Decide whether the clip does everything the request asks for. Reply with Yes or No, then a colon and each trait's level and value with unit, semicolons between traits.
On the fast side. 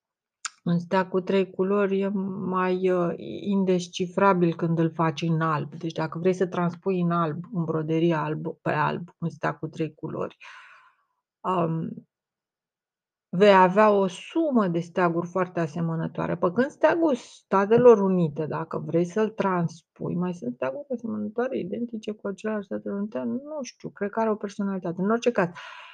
No: average, 155 wpm